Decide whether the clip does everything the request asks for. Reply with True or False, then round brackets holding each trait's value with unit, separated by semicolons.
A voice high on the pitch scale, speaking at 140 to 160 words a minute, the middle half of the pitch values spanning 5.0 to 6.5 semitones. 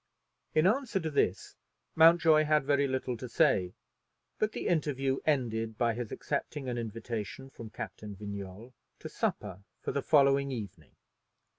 False (130 Hz; 145 wpm; 5.3 semitones)